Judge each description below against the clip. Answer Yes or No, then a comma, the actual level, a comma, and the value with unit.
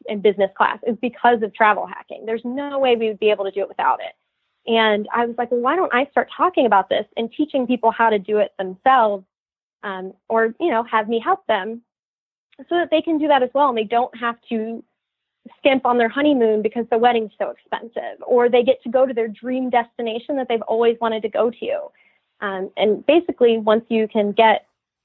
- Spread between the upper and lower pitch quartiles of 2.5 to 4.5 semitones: Yes, average, 3.0 semitones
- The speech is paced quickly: Yes, fast, 225 wpm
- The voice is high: Yes, high, 235 Hz